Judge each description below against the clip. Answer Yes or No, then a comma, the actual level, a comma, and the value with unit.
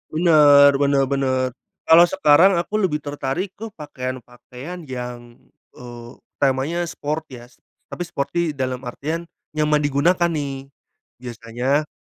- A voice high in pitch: No, medium, 140 Hz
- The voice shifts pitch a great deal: No, average, 3.3 semitones